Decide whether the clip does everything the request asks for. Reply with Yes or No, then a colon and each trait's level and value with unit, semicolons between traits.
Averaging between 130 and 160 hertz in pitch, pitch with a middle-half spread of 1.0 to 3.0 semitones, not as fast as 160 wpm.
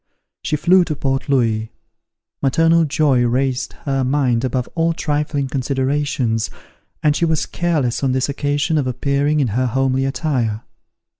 Yes: low, 135 Hz; average, 2.7 semitones; average, 145 wpm